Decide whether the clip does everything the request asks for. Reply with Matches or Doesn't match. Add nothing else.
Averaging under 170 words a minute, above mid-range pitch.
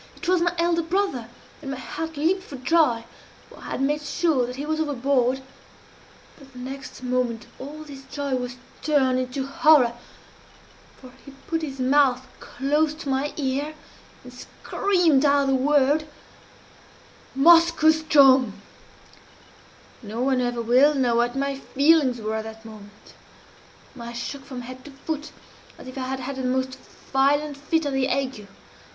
Matches